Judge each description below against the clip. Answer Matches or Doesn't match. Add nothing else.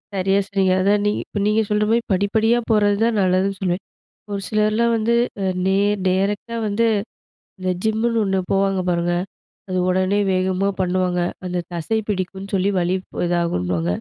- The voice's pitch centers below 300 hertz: Matches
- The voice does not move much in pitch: Matches